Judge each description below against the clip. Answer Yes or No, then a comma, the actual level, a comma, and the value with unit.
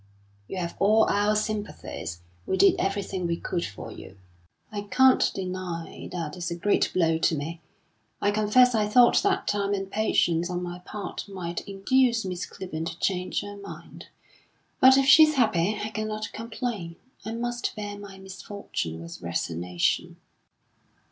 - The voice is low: No, high, 195 Hz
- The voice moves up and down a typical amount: Yes, average, 3.9 semitones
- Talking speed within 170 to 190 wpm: No, average, 155 wpm